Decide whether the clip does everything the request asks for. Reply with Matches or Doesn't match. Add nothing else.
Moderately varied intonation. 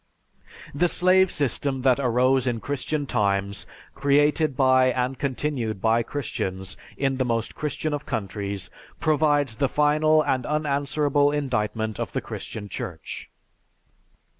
Matches